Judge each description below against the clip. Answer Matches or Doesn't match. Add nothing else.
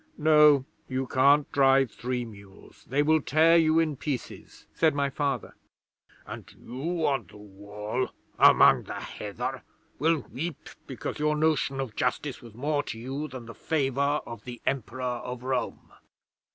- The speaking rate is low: Doesn't match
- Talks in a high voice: Doesn't match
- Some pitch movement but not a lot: Matches